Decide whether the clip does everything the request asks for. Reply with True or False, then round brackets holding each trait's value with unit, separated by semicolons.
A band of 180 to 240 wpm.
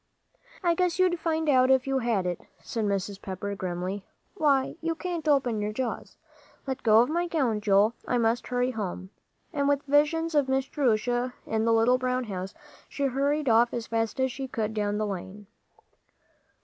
True (185 wpm)